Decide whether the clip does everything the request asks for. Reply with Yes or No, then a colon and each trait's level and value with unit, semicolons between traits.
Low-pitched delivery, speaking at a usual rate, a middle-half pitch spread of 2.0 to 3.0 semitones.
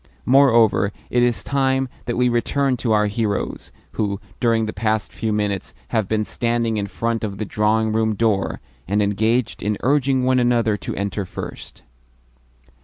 Yes: low, 110 Hz; average, 165 wpm; narrow, 2.6 semitones